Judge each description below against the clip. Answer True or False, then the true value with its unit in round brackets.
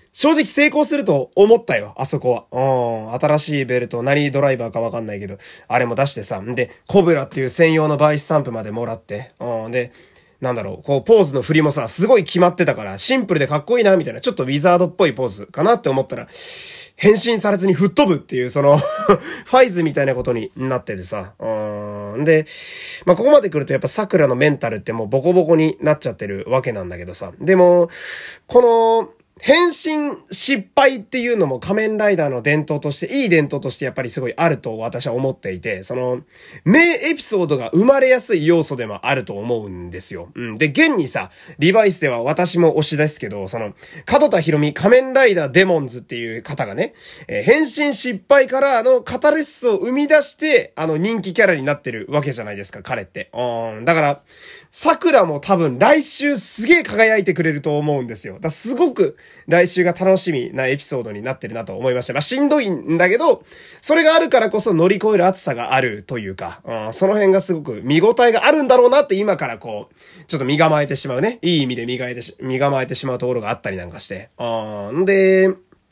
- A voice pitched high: False (160 Hz)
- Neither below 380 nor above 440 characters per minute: True (425 characters per minute)